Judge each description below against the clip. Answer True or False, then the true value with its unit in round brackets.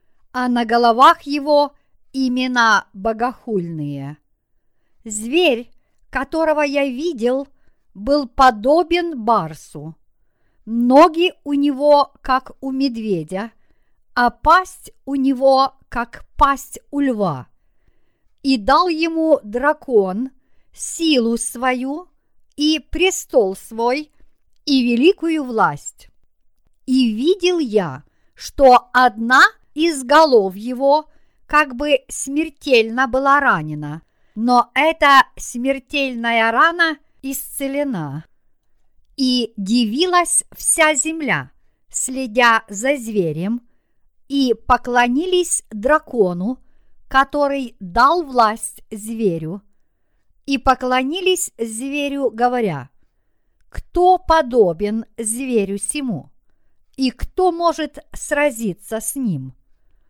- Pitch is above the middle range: True (255 Hz)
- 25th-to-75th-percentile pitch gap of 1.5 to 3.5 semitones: False (4.6 semitones)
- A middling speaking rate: False (85 wpm)